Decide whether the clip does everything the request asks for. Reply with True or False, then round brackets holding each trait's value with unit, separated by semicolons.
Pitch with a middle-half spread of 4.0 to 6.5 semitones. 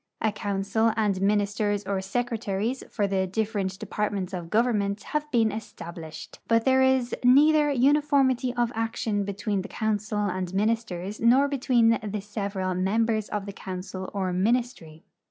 False (3.3 semitones)